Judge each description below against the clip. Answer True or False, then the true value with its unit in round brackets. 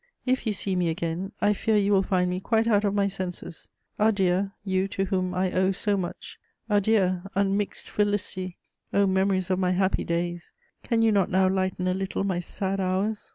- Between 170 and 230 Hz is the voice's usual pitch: True (190 Hz)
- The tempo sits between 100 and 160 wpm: False (195 wpm)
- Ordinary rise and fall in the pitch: False (1.7 semitones)